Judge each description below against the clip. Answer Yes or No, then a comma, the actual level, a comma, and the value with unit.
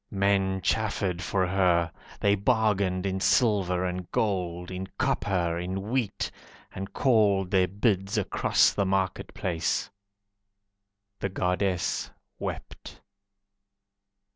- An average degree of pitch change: No, narrow, 1.8 semitones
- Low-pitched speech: Yes, very low, 95 Hz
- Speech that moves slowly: Yes, slow, 105 wpm